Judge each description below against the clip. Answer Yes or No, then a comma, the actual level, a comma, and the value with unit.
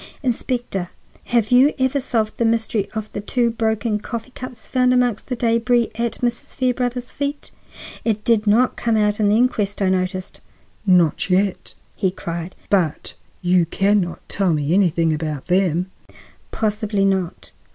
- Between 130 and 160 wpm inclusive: Yes, average, 150 wpm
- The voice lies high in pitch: Yes, high, 215 Hz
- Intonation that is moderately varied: Yes, average, 4.3 semitones